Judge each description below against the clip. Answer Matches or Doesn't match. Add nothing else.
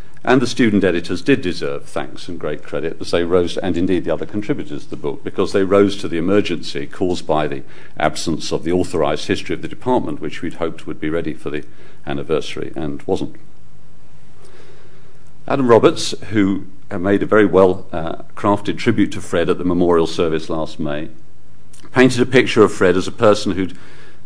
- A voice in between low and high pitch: Doesn't match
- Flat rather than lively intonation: Doesn't match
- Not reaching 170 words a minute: Doesn't match